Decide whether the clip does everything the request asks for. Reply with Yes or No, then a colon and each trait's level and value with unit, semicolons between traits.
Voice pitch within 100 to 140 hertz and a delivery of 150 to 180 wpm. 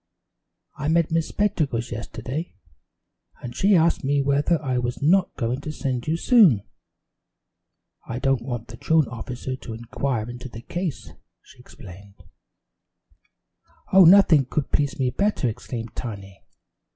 No: low, 135 Hz; average, 140 wpm